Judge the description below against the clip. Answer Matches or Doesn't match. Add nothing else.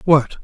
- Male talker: Matches